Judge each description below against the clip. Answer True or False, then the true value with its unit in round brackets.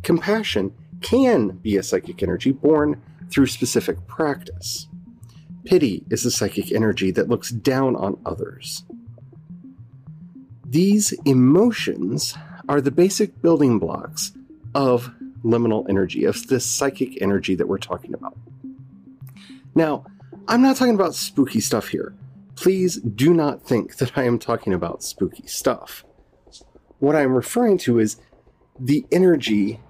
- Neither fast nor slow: False (130 wpm)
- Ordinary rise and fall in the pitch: False (6.7 semitones)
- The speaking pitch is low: True (130 Hz)